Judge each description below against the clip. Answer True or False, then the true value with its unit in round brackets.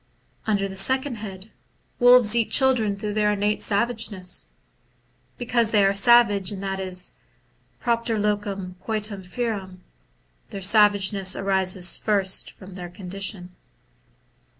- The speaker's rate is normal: False (125 wpm)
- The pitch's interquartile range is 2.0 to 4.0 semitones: True (2.6 semitones)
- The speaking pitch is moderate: False (205 Hz)